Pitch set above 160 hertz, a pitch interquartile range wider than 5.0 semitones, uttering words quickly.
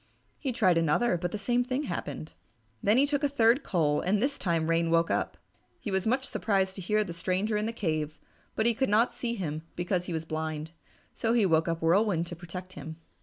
Yes: high, 190 Hz; wide, 5.6 semitones; fast, 220 wpm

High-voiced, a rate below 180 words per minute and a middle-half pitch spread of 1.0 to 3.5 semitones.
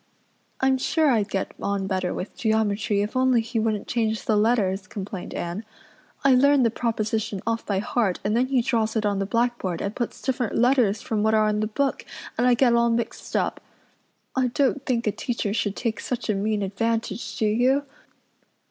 No: high, 225 Hz; average, 195 wpm; average, 2.9 semitones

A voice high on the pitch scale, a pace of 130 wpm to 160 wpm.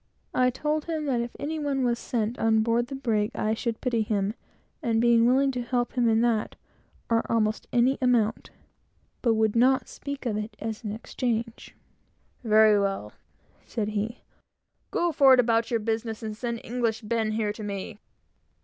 No: high, 230 Hz; average, 175 wpm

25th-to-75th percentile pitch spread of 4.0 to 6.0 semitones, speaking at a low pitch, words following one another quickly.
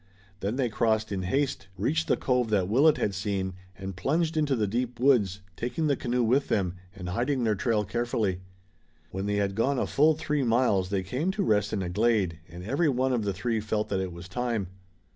Yes: average, 4.8 semitones; low, 110 Hz; fast, 215 wpm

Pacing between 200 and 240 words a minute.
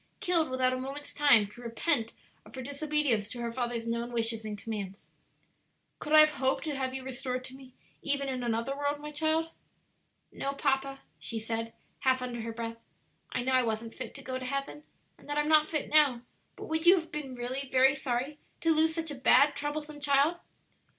Yes: fast, 205 wpm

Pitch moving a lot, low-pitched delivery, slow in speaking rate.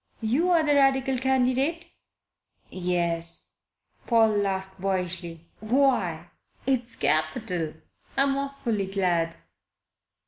No: wide, 7.1 semitones; high, 215 Hz; slow, 80 wpm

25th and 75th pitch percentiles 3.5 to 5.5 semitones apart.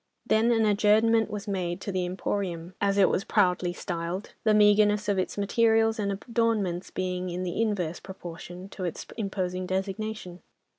No: average, 2.8 semitones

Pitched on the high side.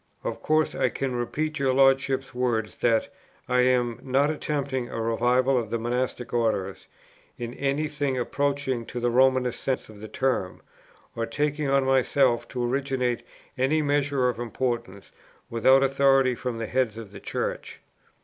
No: low, 130 Hz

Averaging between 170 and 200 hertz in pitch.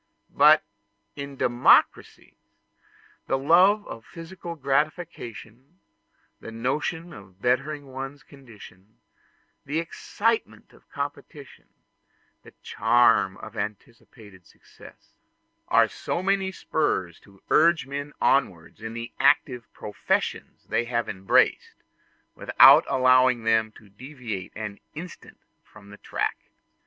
No: low, 130 Hz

